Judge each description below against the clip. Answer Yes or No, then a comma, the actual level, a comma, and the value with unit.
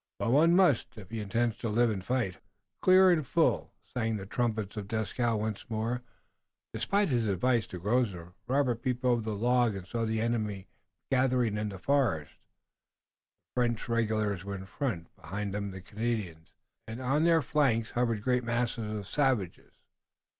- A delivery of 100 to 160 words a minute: No, average, 170 wpm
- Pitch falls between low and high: No, low, 115 Hz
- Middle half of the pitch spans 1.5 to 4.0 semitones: Yes, average, 3.4 semitones